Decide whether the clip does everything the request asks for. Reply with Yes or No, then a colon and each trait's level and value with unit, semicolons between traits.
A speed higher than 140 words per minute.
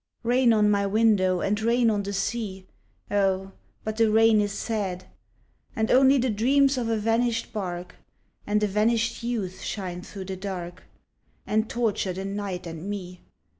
Yes: average, 165 wpm